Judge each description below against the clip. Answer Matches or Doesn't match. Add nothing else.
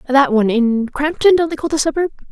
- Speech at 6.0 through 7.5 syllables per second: Matches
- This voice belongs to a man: Doesn't match